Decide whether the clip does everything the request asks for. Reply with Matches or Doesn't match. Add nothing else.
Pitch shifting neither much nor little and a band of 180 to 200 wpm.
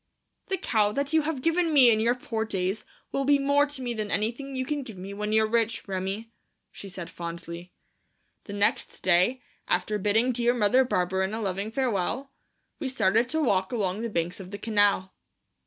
Matches